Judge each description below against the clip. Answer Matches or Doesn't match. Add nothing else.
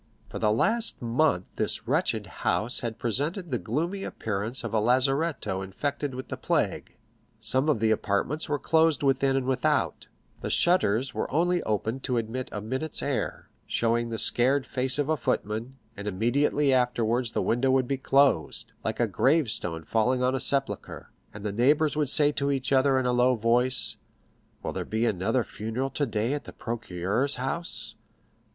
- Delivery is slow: Doesn't match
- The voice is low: Matches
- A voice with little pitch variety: Doesn't match